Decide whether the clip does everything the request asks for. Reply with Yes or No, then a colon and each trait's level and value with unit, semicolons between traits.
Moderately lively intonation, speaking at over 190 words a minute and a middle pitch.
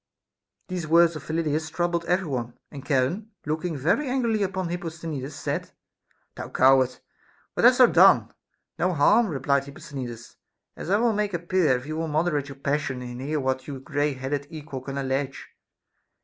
No: average, 4.3 semitones; average, 175 wpm; medium, 150 Hz